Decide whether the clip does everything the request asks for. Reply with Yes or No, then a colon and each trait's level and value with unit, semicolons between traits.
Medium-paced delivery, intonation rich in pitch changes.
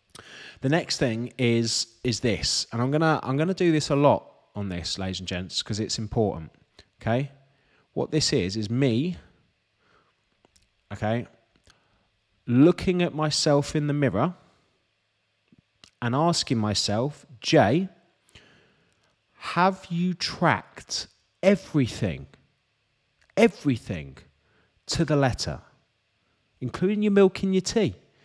No: slow, 120 wpm; wide, 6.4 semitones